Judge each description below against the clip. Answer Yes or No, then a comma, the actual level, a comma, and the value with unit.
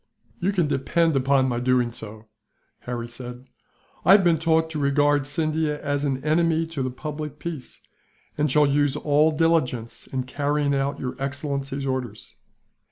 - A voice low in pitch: No, medium, 145 Hz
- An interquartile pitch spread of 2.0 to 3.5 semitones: Yes, average, 2.9 semitones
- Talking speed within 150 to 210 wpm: Yes, average, 160 wpm